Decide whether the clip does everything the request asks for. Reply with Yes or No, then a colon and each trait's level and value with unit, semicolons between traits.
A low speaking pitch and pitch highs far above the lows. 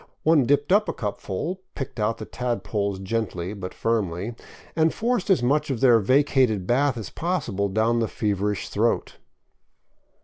Yes: low, 115 Hz; wide, 5.9 semitones